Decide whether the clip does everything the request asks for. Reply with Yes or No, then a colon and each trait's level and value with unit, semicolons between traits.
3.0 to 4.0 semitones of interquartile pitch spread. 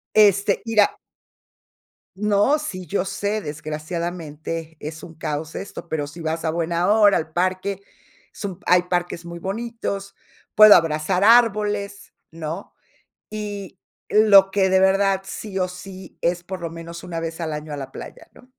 Yes: average, 3.5 semitones